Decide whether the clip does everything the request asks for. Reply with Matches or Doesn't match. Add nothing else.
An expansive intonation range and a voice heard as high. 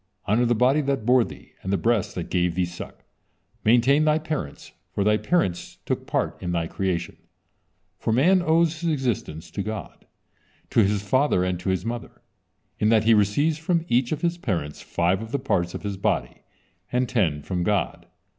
Doesn't match